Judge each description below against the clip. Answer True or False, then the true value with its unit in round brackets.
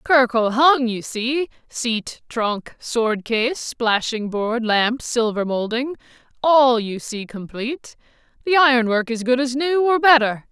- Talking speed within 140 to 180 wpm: True (145 wpm)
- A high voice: True (245 Hz)